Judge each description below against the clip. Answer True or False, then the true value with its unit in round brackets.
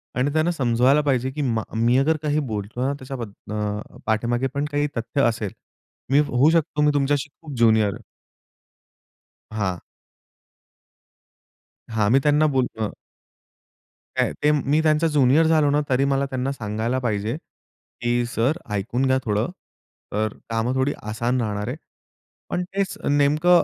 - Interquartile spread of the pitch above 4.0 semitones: True (4.6 semitones)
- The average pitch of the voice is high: False (130 Hz)